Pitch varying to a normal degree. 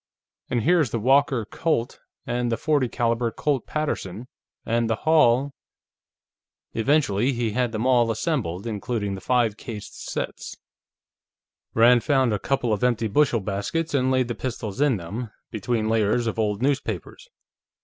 Yes: average, 3.5 semitones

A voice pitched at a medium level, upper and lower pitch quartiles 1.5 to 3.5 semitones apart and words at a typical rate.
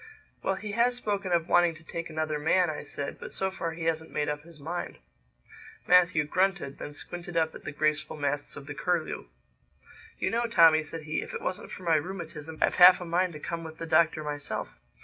No: medium, 165 Hz; average, 2.9 semitones; fast, 215 wpm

